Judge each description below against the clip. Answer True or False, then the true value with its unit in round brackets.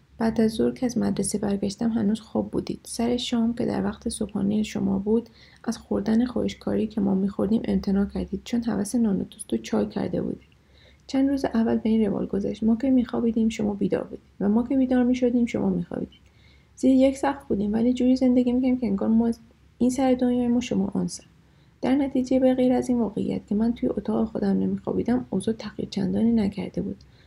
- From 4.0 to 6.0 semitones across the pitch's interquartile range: False (3.2 semitones)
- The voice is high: True (225 Hz)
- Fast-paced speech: True (195 wpm)